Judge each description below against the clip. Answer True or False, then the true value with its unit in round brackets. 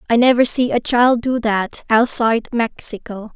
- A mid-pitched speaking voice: False (235 Hz)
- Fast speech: False (160 wpm)